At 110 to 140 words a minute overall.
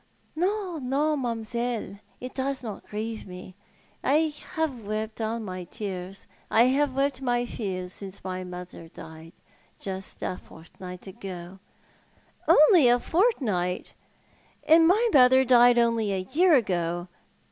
Yes: slow, 135 wpm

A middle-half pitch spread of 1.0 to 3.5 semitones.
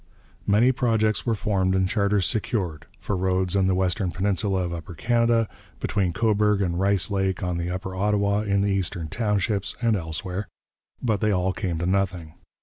Yes: narrow, 2.4 semitones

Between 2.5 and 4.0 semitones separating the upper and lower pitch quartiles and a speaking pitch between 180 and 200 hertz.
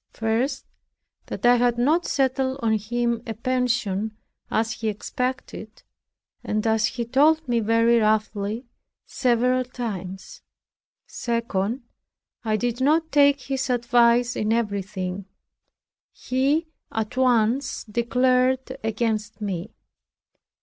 No: average, 2.9 semitones; high, 235 Hz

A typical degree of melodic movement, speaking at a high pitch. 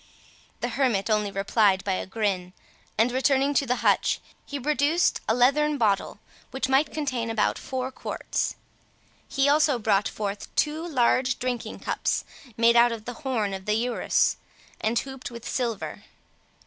Yes: average, 4.1 semitones; high, 245 Hz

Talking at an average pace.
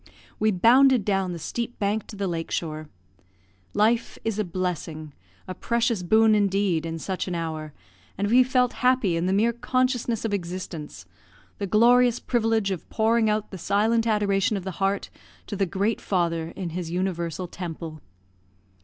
Yes: average, 165 wpm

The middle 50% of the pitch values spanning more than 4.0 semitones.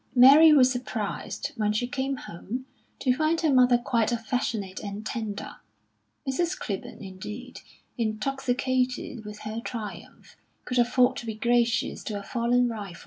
No: average, 3.1 semitones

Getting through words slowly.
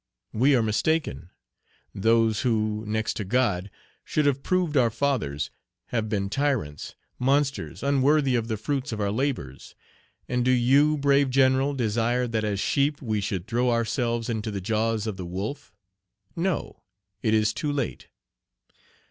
No: average, 150 wpm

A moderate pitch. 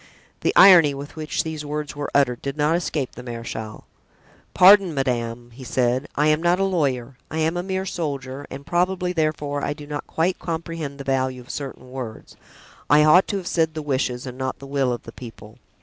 Yes: medium, 145 Hz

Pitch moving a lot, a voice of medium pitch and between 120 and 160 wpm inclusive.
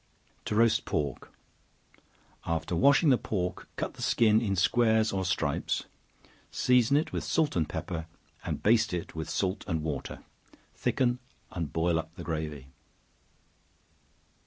No: wide, 6.1 semitones; very low, 95 Hz; slow, 135 wpm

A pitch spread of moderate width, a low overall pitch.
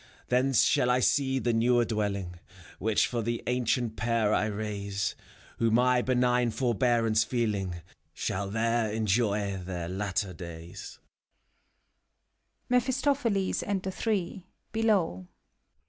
Yes: average, 3.3 semitones; low, 110 Hz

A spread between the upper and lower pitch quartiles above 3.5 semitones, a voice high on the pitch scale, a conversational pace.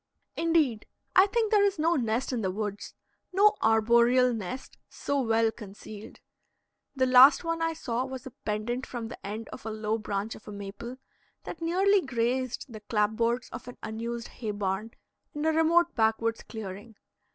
Yes: average, 4.4 semitones; high, 235 Hz; average, 170 wpm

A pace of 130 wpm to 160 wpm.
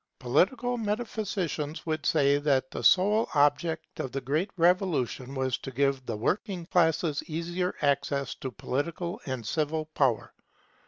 Yes: average, 140 wpm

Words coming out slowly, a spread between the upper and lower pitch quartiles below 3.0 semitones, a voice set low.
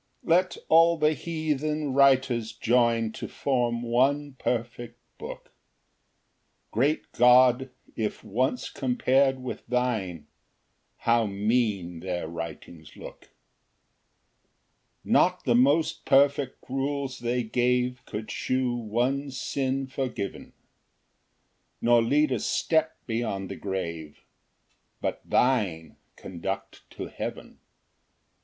No: slow, 105 wpm; average, 3.5 semitones; low, 125 Hz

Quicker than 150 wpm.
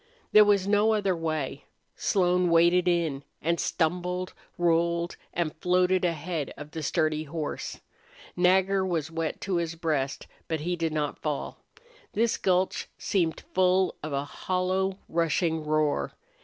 No: average, 140 wpm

